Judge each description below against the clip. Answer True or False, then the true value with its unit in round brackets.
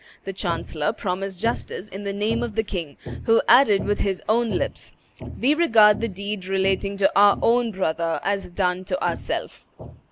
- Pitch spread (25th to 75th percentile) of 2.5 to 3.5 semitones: True (2.8 semitones)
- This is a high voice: True (200 Hz)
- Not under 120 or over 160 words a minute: False (170 wpm)